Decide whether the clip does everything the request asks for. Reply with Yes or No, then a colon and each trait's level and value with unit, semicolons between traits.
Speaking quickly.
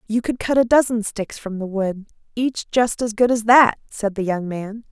Yes: fast, 230 wpm